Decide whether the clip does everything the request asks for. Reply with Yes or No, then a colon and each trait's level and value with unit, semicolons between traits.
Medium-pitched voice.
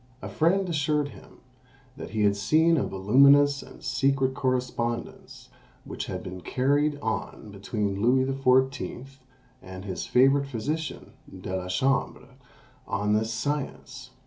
No: low, 130 Hz